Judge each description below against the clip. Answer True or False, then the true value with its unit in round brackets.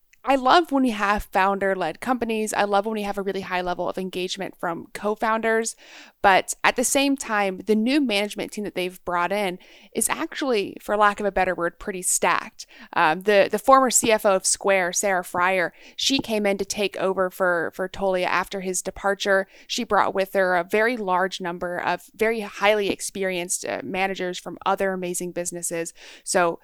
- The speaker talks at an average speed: True (185 wpm)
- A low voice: False (195 Hz)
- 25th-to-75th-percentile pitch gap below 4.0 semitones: True (2.9 semitones)